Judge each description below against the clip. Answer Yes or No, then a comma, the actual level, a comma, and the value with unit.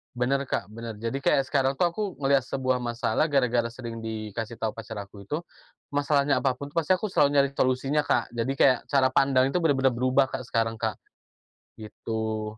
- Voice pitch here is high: No, low, 130 Hz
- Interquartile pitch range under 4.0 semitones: Yes, average, 3.3 semitones